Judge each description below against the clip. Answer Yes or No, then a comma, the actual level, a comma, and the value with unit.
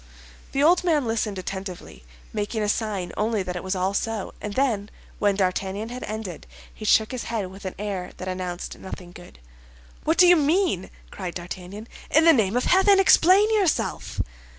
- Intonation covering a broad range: Yes, wide, 6.4 semitones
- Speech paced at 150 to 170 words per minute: No, average, 180 wpm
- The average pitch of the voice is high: Yes, high, 210 Hz